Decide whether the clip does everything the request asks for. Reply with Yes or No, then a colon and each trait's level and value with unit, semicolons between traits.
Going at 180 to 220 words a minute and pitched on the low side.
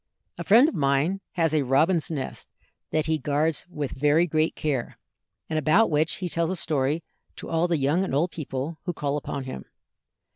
No: average, 190 wpm; medium, 155 Hz